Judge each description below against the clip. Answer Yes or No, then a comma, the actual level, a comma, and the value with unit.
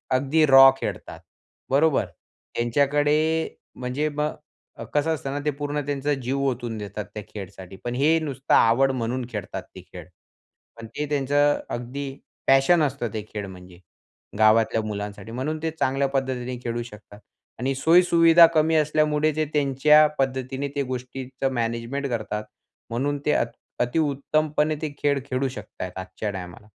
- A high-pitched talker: No, low, 135 Hz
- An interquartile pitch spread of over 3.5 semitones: Yes, average, 4.0 semitones